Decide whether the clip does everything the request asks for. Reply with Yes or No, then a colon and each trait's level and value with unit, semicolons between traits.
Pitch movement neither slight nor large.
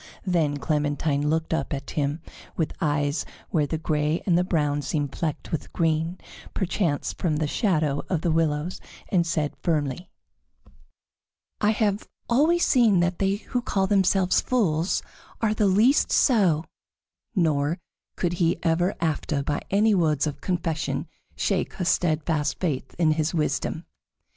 Yes: average, 3.8 semitones